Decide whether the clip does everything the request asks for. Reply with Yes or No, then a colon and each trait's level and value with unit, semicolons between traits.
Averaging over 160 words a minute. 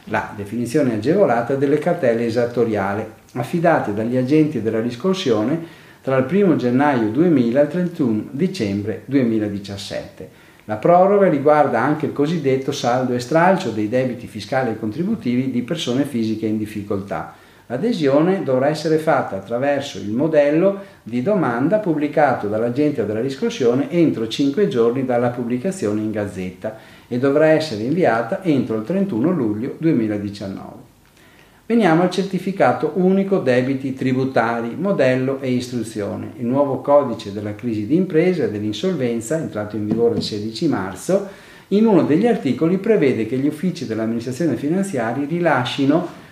No: average, 135 wpm